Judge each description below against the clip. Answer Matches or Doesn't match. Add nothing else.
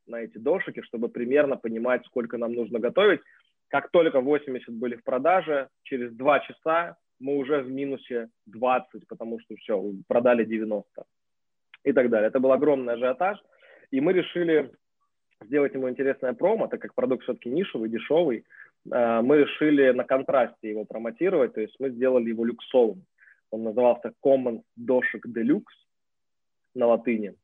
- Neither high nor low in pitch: Doesn't match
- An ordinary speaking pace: Matches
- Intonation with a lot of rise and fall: Doesn't match